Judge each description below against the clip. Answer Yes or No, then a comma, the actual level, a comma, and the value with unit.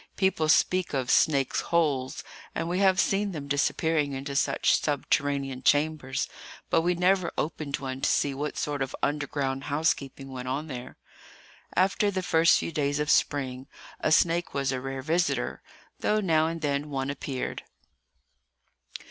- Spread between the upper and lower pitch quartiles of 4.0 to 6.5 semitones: No, average, 3.5 semitones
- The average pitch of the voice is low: No, medium, 145 Hz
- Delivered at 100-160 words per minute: Yes, average, 155 wpm